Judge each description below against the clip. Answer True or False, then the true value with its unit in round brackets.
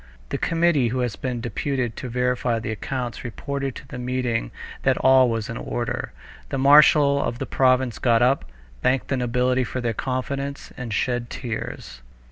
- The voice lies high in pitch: False (125 Hz)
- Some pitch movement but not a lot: False (2.1 semitones)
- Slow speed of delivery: False (170 wpm)